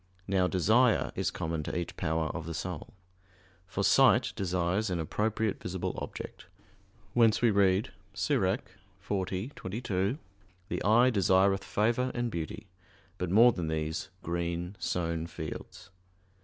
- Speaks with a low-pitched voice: Yes, very low, 95 Hz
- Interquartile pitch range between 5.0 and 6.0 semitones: No, average, 4.2 semitones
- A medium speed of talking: No, slow, 130 wpm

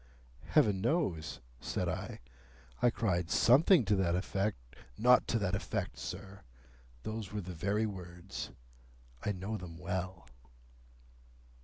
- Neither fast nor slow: No, slow, 125 wpm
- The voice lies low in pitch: Yes, very low, 95 Hz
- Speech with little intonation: No, average, 3.4 semitones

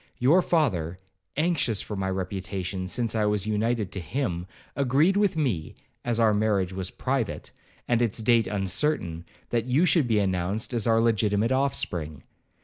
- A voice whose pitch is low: Yes, low, 110 Hz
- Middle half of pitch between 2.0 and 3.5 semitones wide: No, average, 4.8 semitones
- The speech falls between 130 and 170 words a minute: Yes, average, 155 wpm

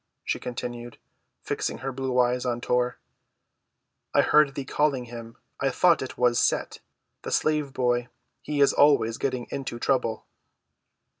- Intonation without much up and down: Yes, narrow, 2.1 semitones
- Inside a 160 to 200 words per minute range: No, average, 145 wpm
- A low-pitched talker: Yes, low, 125 Hz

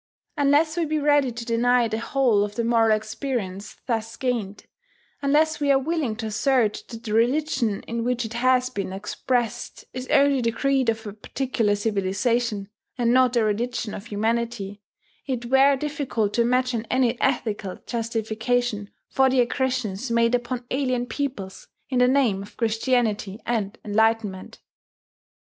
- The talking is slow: No, average, 155 wpm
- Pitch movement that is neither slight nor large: Yes, average, 3.0 semitones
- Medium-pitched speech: No, high, 235 Hz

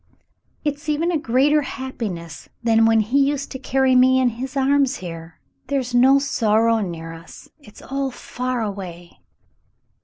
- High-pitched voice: Yes, very high, 255 Hz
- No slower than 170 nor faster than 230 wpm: No, average, 150 wpm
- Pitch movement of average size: Yes, average, 4.5 semitones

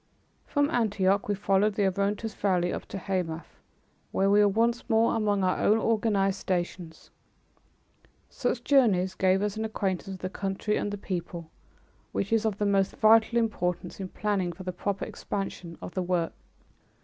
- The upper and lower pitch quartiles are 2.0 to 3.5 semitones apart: Yes, narrow, 2.6 semitones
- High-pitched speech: Yes, high, 200 Hz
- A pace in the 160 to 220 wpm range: Yes, average, 170 wpm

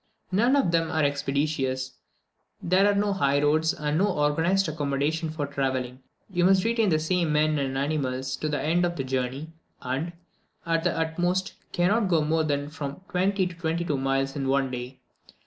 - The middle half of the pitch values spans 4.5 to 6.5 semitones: No, average, 4.1 semitones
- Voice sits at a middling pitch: Yes, medium, 155 Hz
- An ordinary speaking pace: Yes, average, 180 wpm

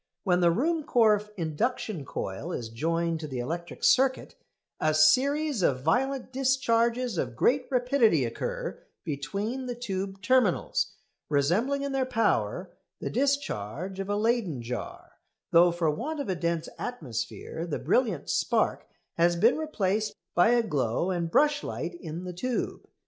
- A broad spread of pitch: Yes, wide, 7.7 semitones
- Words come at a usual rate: Yes, average, 145 wpm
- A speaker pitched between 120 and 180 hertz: No, high, 190 Hz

